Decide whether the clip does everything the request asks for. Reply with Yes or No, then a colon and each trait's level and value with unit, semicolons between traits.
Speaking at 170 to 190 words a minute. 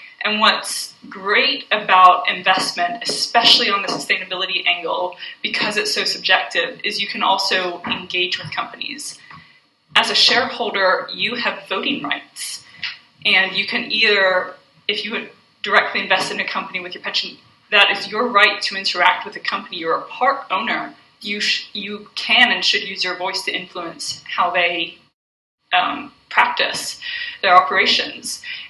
No: average, 155 wpm